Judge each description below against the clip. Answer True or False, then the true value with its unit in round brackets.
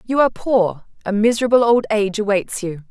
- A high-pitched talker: True (215 Hz)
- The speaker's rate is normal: True (185 wpm)